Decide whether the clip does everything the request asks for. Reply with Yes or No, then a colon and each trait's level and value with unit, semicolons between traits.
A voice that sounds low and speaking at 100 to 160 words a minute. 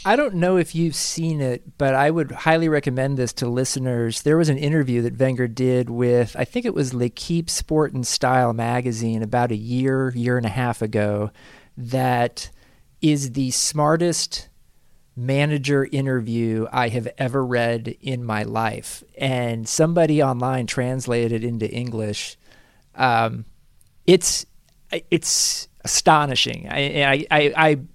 Yes: low, 130 Hz; average, 150 wpm